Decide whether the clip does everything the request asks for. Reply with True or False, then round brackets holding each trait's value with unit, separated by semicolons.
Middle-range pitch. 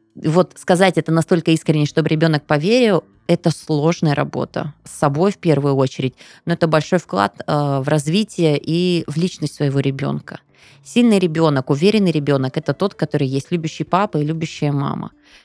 True (160 Hz)